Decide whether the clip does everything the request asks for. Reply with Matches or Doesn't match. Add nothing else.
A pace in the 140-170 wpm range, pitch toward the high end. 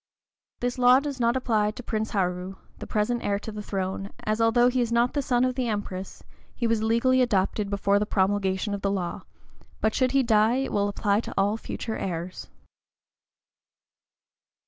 Doesn't match